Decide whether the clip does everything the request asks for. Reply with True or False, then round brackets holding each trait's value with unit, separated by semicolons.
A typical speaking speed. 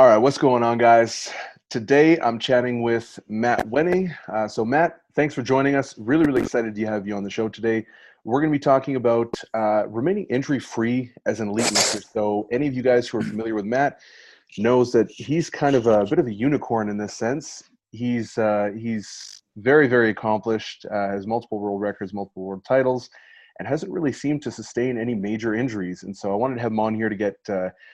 False (215 wpm)